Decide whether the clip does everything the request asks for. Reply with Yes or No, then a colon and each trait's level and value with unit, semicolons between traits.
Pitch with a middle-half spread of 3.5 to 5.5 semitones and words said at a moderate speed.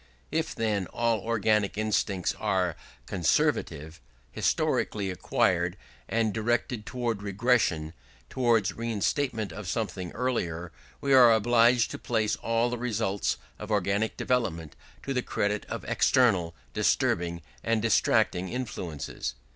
No: average, 4.0 semitones; slow, 115 wpm